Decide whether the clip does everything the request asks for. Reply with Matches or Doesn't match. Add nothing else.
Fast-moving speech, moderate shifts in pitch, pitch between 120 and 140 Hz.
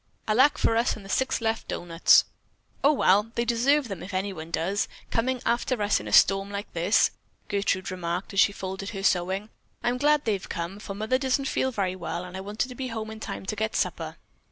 Doesn't match